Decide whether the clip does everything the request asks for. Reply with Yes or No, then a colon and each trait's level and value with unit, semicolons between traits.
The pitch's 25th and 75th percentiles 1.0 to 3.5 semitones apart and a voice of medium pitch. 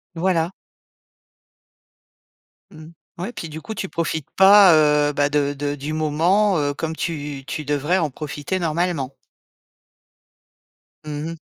Yes: average, 2.9 semitones; medium, 155 Hz